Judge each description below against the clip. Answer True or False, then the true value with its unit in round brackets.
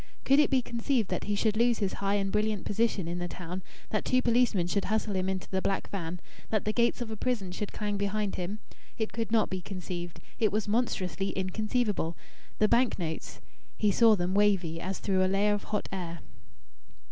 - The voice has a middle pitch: False (205 Hz)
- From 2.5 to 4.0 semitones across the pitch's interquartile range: True (2.8 semitones)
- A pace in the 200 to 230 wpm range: True (205 wpm)